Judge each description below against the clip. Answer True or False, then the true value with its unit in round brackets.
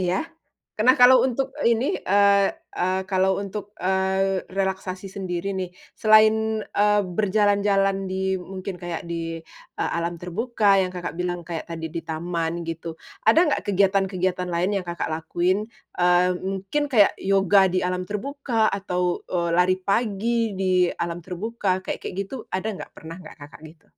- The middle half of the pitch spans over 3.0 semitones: False (2.4 semitones)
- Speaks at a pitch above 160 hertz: True (190 Hz)